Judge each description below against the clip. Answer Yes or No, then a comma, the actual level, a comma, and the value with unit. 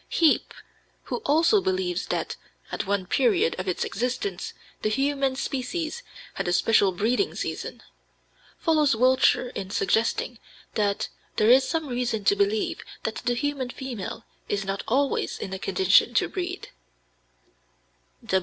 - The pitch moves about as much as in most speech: No, wide, 5.9 semitones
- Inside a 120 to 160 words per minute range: Yes, slow, 135 wpm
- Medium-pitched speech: No, high, 245 Hz